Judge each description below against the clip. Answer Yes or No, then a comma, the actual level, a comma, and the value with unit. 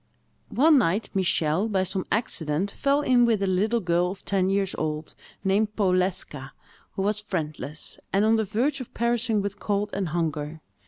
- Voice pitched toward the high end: Yes, high, 195 Hz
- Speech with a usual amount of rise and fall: Yes, average, 4.0 semitones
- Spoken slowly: No, average, 170 wpm